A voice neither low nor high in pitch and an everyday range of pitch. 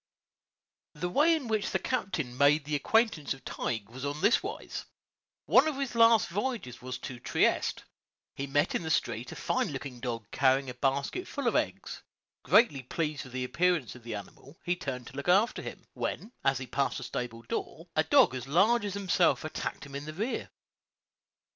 No: medium, 145 Hz; wide, 8.0 semitones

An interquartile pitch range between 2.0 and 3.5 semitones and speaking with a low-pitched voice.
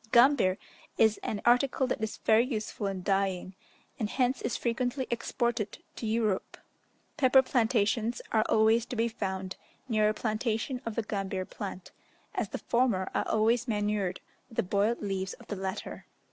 No: average, 3.1 semitones; high, 220 Hz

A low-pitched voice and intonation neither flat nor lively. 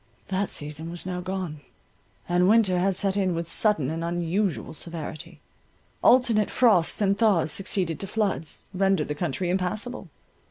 No: medium, 185 Hz; average, 3.0 semitones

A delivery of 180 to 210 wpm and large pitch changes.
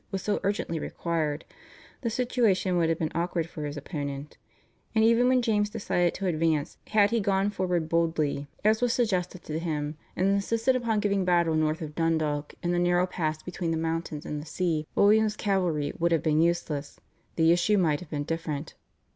No: average, 190 wpm; average, 4.2 semitones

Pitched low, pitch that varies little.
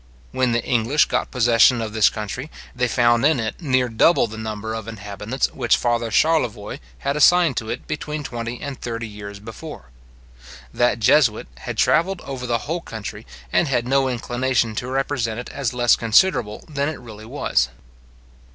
No: low, 120 Hz; average, 3.6 semitones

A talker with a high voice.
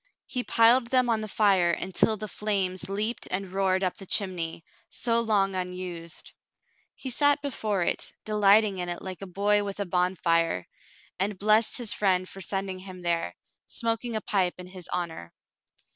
Yes: high, 195 Hz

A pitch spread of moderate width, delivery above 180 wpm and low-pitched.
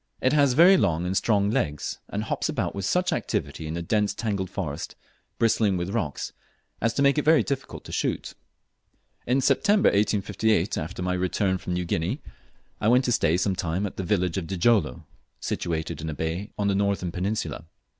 Yes: average, 4.9 semitones; average, 190 wpm; low, 100 Hz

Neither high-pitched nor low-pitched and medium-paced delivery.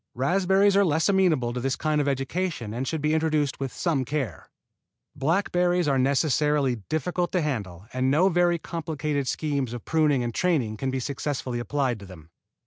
Yes: medium, 145 Hz; average, 175 wpm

